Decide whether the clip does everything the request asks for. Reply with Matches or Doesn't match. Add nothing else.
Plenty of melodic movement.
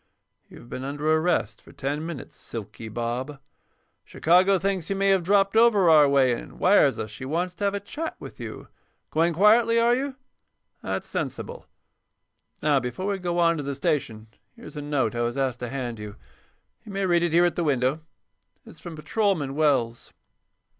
Matches